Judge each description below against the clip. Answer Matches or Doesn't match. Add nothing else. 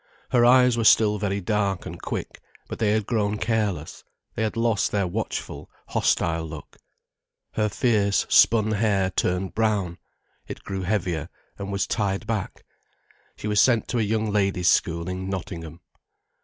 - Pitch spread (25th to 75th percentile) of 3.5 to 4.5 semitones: Doesn't match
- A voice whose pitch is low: Matches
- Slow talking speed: Doesn't match